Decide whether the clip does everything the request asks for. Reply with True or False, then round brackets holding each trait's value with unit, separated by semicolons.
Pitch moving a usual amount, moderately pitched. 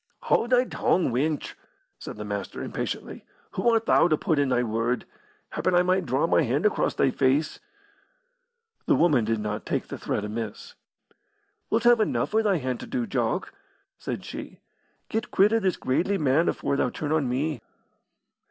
False (7.7 semitones; 150 Hz)